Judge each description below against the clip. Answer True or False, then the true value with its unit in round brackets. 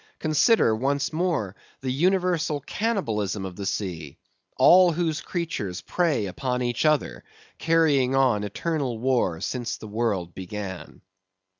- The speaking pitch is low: True (130 Hz)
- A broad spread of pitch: True (7.6 semitones)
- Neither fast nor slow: False (125 wpm)